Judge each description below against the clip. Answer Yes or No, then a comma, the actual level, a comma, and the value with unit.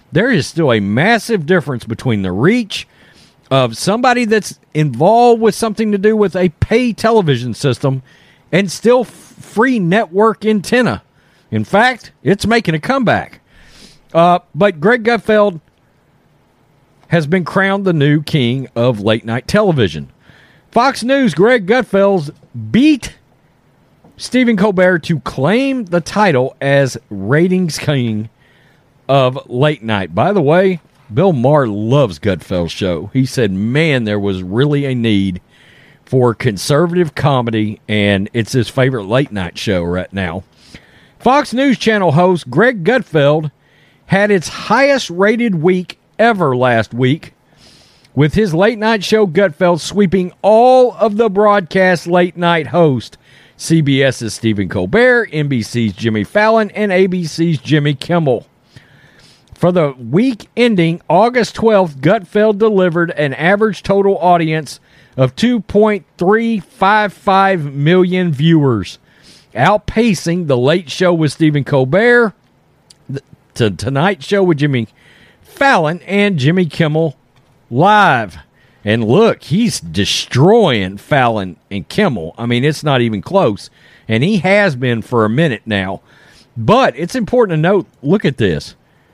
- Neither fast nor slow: No, slow, 130 wpm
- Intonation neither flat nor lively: No, wide, 8.0 semitones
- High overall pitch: No, medium, 165 Hz